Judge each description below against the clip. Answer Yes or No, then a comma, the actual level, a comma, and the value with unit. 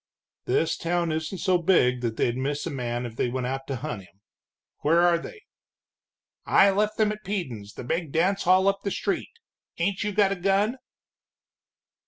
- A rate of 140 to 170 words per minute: No, average, 185 wpm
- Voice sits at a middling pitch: Yes, medium, 170 Hz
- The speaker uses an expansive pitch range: Yes, wide, 7.4 semitones